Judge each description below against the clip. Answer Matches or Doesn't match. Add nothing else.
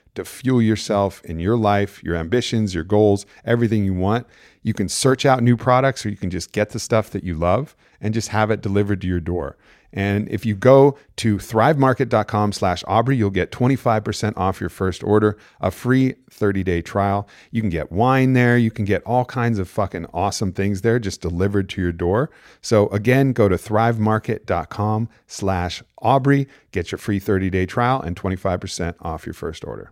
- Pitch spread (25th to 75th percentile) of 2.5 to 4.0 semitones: Matches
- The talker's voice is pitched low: Matches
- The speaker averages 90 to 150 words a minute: Doesn't match